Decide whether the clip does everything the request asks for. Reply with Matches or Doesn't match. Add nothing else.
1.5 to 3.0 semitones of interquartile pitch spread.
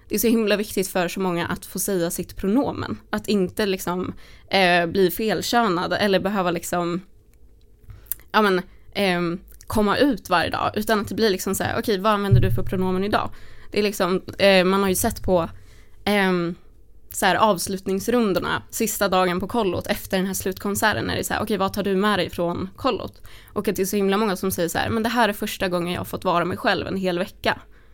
Matches